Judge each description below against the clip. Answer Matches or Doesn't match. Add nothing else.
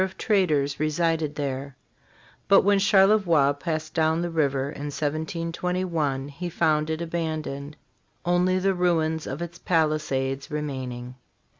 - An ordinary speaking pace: Doesn't match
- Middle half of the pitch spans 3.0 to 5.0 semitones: Matches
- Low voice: Doesn't match